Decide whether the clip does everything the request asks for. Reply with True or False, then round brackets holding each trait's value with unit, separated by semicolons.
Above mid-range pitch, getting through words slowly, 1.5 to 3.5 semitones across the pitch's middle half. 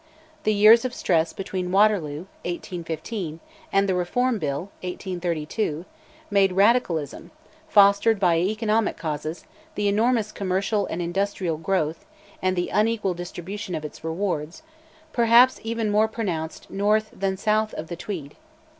False (195 Hz; 130 wpm; 4.0 semitones)